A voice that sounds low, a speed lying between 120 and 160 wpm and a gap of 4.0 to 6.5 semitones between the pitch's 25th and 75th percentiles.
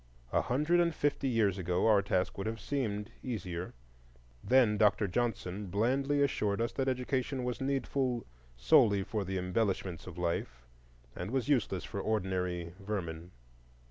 Yes: low, 105 Hz; average, 145 wpm; wide, 5.6 semitones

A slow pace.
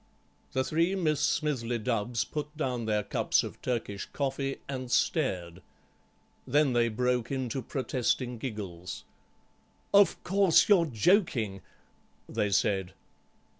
Yes: slow, 115 wpm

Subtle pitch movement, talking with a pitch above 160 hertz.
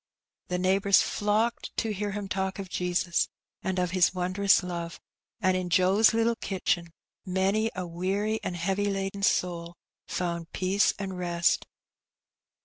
Yes: narrow, 2.0 semitones; high, 190 Hz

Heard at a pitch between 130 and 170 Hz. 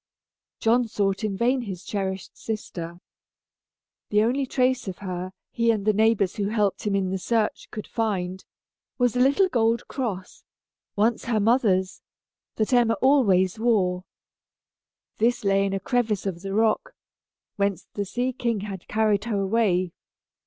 No: high, 210 Hz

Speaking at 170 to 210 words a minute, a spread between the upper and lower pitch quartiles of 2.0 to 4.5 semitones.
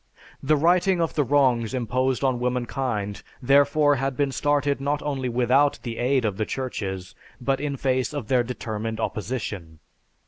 No: average, 160 wpm; average, 3.2 semitones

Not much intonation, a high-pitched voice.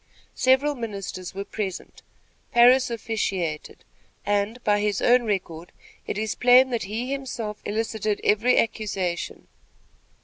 No: average, 3.5 semitones; high, 215 Hz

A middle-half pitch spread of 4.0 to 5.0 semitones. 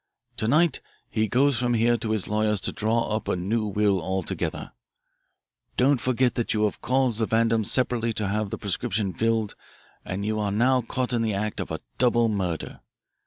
No: narrow, 2.4 semitones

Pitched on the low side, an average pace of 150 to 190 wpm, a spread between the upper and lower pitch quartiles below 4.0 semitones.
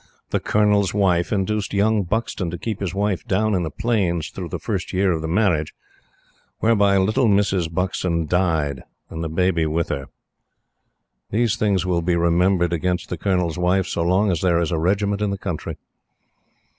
Yes: very low, 90 Hz; average, 180 wpm; average, 3.1 semitones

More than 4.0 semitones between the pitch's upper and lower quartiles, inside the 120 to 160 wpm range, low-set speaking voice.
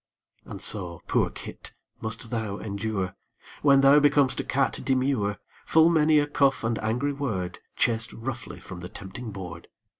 Yes: wide, 5.6 semitones; average, 155 wpm; low, 115 Hz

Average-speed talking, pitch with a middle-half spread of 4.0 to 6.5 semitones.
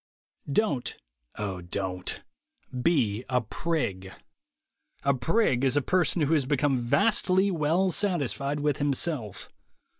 No: slow, 115 wpm; wide, 5.6 semitones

